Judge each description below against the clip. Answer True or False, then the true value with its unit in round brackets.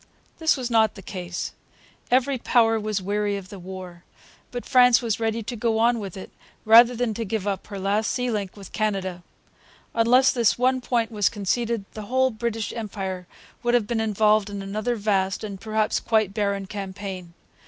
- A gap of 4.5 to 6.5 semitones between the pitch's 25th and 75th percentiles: False (3.0 semitones)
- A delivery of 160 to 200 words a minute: True (180 wpm)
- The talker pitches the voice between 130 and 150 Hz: False (215 Hz)